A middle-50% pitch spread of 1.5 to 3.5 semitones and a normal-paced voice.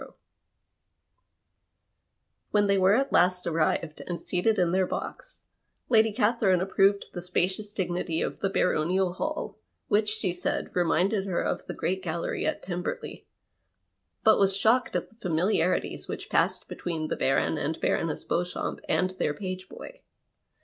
Yes: average, 2.9 semitones; average, 145 wpm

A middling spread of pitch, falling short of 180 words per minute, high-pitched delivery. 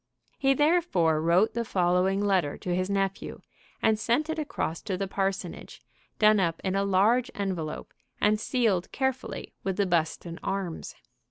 Yes: average, 3.6 semitones; average, 155 wpm; high, 195 Hz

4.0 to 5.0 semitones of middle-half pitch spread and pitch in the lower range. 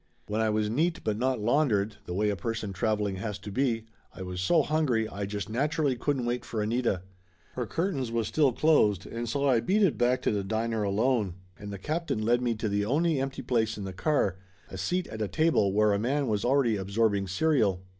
Yes: average, 4.6 semitones; low, 115 Hz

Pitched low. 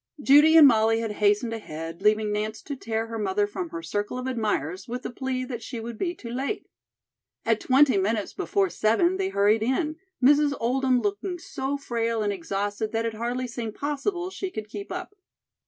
No: high, 230 Hz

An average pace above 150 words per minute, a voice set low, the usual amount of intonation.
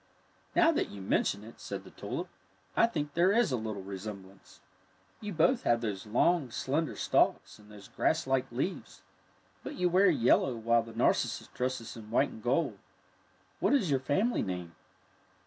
No: average, 170 wpm; low, 125 Hz; wide, 8.1 semitones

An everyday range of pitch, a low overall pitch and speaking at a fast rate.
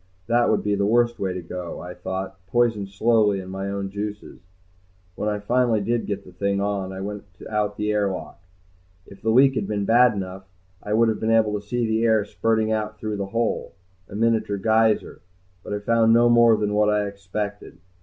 No: narrow, 2.2 semitones; low, 105 Hz; fast, 210 wpm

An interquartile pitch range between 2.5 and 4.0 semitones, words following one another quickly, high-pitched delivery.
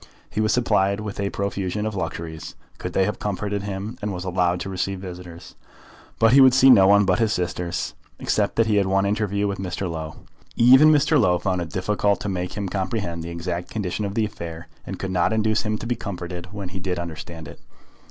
No: average, 2.9 semitones; fast, 220 wpm; very low, 95 Hz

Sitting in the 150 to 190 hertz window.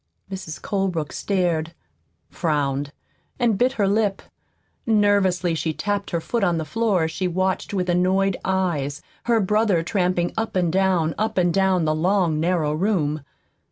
Yes: medium, 185 Hz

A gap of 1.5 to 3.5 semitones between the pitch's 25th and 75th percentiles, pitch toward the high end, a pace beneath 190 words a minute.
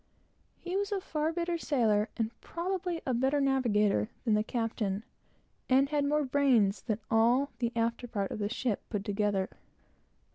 No: wide, 5.6 semitones; high, 245 Hz; average, 160 wpm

